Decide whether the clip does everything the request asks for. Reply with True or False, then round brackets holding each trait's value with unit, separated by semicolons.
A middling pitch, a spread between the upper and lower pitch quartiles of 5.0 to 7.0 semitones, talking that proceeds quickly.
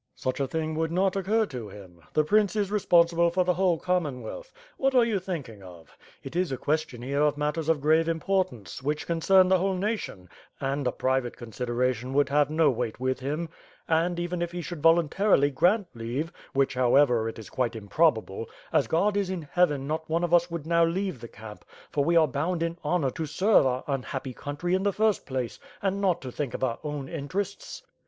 True (155 Hz; 5.4 semitones; 220 wpm)